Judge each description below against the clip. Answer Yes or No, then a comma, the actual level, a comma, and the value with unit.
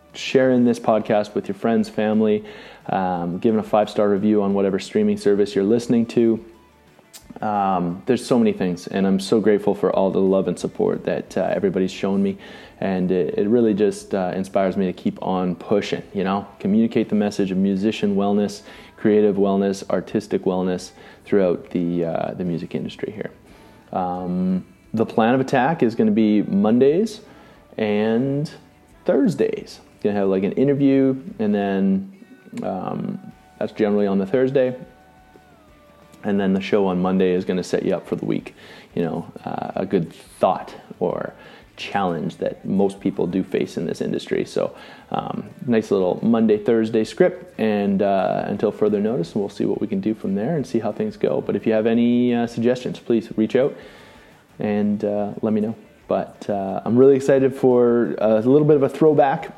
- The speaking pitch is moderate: No, low, 105 Hz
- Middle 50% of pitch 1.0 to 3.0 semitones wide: No, average, 3.7 semitones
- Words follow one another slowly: No, average, 180 wpm